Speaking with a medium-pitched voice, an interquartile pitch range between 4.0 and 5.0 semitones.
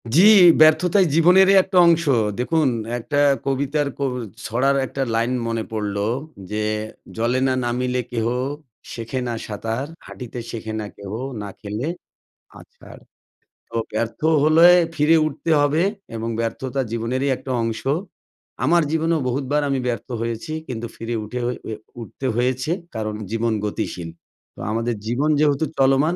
No: low, 125 Hz; average, 4.6 semitones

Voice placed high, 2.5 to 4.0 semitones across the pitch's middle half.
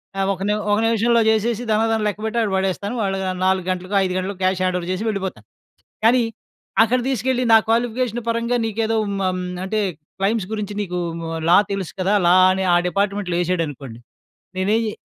Yes: high, 205 Hz; average, 3.3 semitones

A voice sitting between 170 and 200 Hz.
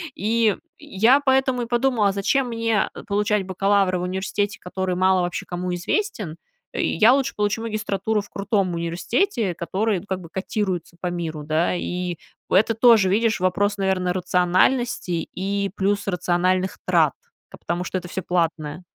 Yes: high, 190 Hz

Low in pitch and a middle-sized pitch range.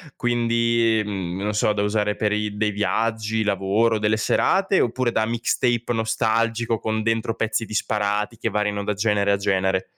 No: low, 110 Hz; narrow, 1.8 semitones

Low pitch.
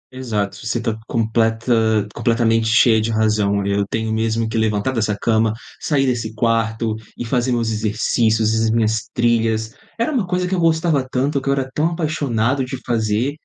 Yes: low, 115 Hz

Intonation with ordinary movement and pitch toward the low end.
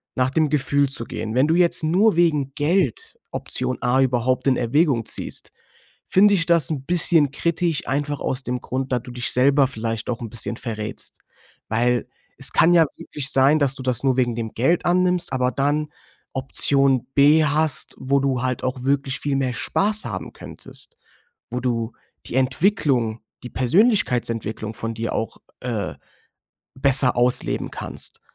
Yes: average, 3.5 semitones; low, 130 Hz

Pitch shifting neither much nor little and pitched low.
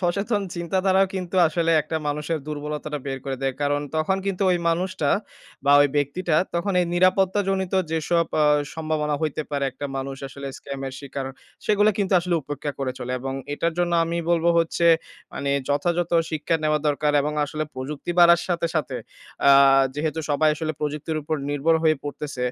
No: average, 3.2 semitones; medium, 155 Hz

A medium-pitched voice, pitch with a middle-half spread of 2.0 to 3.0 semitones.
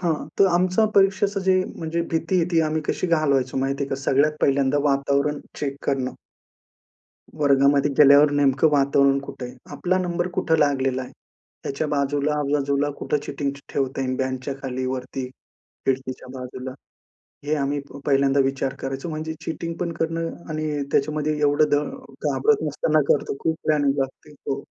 Yes: medium, 145 Hz; average, 2.7 semitones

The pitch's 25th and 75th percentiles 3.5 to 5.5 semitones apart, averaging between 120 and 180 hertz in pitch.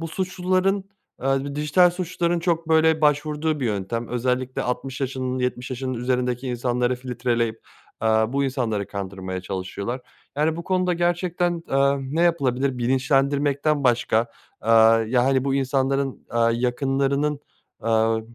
Yes: average, 3.8 semitones; low, 135 Hz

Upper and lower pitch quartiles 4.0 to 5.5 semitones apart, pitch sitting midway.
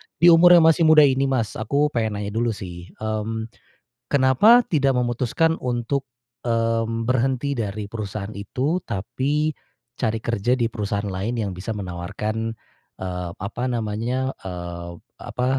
No: average, 4.3 semitones; low, 115 Hz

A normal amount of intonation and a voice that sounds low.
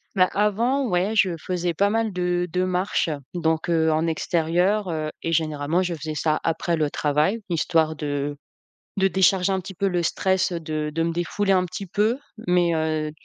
No: average, 3.2 semitones; medium, 175 Hz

